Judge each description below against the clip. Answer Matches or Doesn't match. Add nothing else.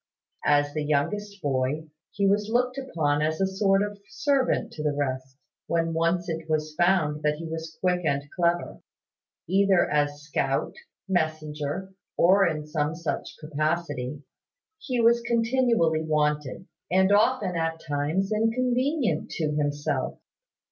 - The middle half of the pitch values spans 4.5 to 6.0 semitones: Matches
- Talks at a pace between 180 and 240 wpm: Doesn't match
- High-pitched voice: Doesn't match